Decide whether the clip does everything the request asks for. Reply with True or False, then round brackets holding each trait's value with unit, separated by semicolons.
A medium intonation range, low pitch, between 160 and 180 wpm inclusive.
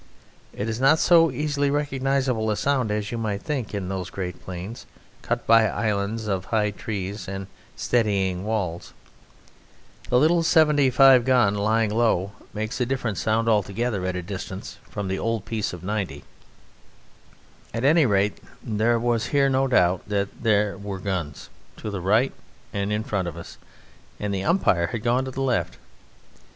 True (4.2 semitones; 110 Hz; 165 wpm)